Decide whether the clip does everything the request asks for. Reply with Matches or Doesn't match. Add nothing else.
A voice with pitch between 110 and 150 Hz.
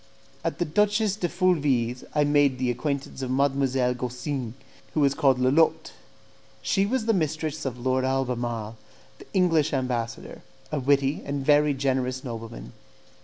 Matches